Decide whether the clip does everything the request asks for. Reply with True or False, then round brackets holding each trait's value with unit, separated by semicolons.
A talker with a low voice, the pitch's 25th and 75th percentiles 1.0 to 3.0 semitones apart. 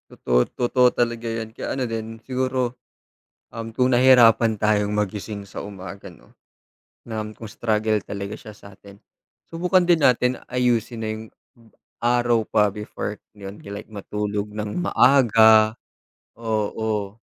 True (110 Hz; 2.7 semitones)